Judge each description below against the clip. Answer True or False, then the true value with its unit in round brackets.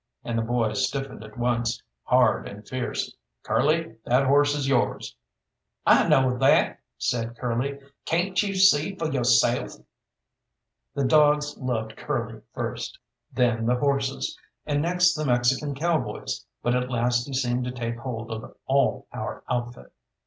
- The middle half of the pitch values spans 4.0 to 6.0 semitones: False (3.3 semitones)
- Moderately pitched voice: False (125 Hz)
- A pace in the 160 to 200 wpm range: False (145 wpm)